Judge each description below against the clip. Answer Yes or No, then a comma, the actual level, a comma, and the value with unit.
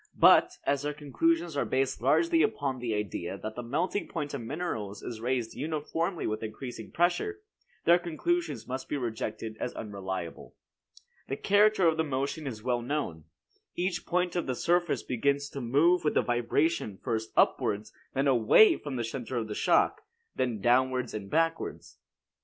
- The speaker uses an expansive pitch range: Yes, wide, 6.3 semitones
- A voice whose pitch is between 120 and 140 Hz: Yes, low, 135 Hz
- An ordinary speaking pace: Yes, average, 165 wpm